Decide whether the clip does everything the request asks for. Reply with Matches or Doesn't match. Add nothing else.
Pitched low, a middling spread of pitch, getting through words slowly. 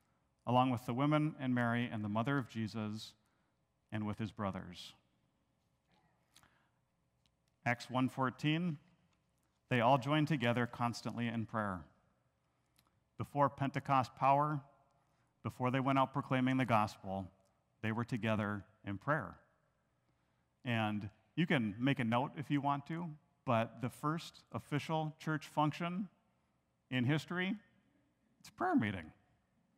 Matches